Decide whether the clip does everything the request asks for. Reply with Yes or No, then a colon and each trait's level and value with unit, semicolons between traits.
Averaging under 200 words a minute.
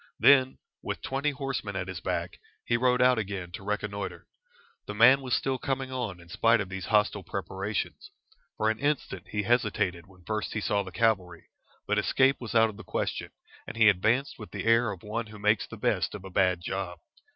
No: fast, 205 wpm